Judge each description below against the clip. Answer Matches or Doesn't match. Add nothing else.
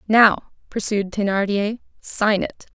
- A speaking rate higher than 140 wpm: Doesn't match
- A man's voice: Doesn't match